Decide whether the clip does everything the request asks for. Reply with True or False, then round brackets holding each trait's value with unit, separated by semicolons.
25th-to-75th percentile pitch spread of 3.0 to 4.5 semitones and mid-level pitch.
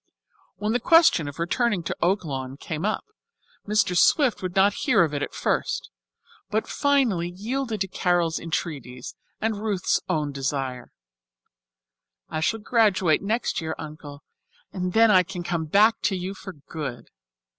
False (5.4 semitones; 180 Hz)